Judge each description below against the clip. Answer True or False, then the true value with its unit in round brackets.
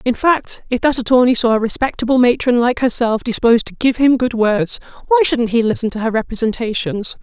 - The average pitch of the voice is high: True (240 Hz)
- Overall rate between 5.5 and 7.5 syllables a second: True (5.7 syllables/s)